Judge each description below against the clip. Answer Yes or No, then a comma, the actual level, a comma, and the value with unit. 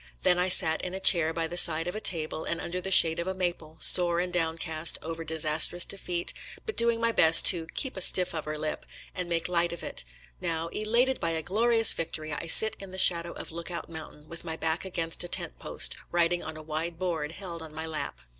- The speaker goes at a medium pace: No, fast, 230 wpm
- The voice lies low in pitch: No, medium, 170 Hz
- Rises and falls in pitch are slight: Yes, narrow, 2.1 semitones